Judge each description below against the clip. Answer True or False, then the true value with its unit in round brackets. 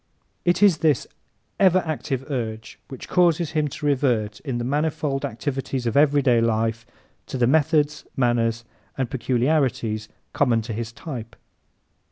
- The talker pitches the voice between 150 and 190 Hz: False (130 Hz)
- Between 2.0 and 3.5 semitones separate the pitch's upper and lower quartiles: False (4.3 semitones)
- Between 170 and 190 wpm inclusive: False (140 wpm)